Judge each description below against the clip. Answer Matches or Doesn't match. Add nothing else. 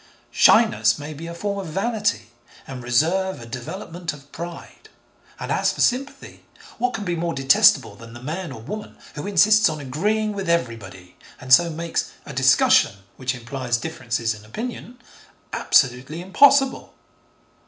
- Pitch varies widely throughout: Matches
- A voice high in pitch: Doesn't match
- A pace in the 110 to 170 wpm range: Matches